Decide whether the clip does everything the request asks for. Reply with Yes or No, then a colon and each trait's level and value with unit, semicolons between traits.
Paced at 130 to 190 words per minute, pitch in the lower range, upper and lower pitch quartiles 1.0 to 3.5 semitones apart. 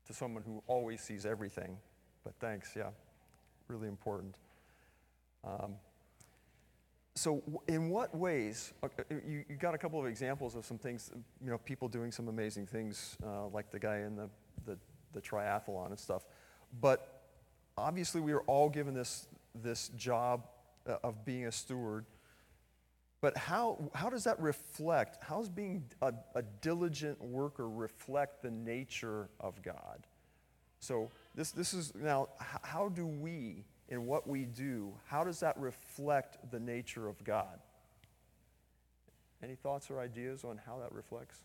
No: average, 150 wpm; low, 120 Hz; average, 5.0 semitones